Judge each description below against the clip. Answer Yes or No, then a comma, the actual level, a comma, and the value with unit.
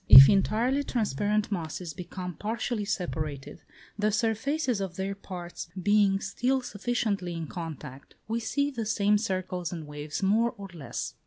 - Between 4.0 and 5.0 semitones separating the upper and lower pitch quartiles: Yes, average, 4.3 semitones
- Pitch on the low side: No, high, 200 Hz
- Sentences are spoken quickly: No, average, 145 wpm